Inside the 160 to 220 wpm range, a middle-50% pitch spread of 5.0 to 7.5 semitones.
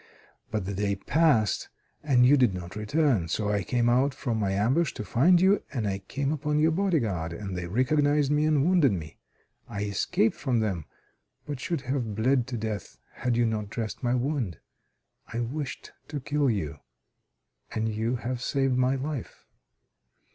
Yes: average, 175 wpm; wide, 5.5 semitones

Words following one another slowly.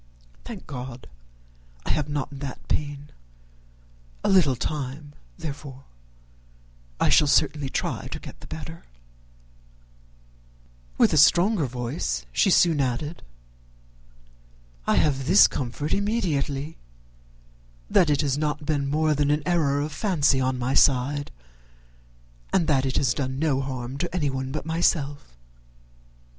Yes: slow, 130 wpm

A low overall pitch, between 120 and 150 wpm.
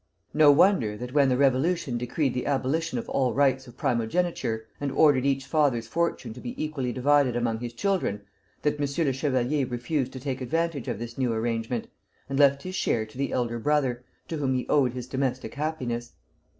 No: low, 130 Hz; average, 190 wpm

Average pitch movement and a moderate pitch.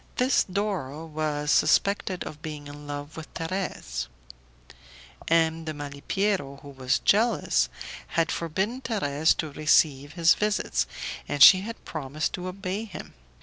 Yes: average, 4.8 semitones; medium, 160 Hz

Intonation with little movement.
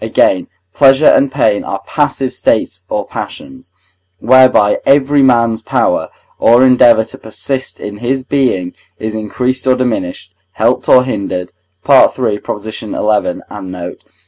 No: average, 4.1 semitones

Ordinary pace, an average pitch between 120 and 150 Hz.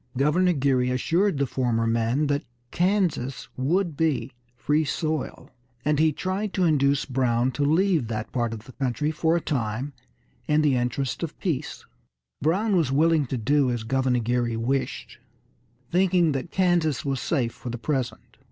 Yes: average, 160 wpm; medium, 140 Hz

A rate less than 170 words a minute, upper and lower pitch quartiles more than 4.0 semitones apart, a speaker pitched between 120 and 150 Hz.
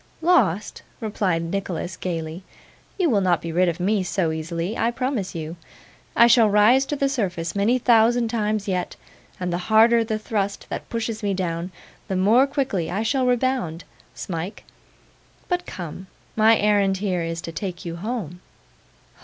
No: average, 160 wpm; average, 4.7 semitones; high, 200 Hz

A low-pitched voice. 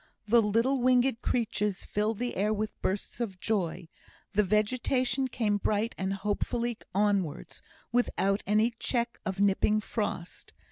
No: high, 215 Hz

